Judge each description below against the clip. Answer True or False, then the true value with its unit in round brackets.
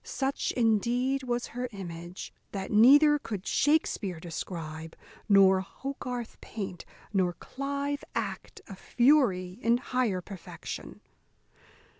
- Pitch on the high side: True (225 Hz)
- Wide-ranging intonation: True (5.9 semitones)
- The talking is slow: True (105 wpm)